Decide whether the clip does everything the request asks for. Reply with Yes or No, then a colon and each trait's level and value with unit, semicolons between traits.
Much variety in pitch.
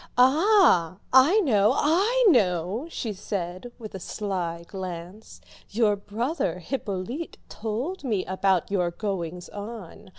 Yes: wide, 6.0 semitones